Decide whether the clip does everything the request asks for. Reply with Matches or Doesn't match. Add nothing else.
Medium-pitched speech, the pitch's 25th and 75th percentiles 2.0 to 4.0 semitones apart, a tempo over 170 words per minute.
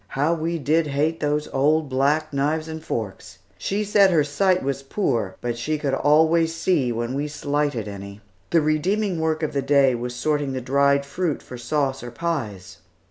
Matches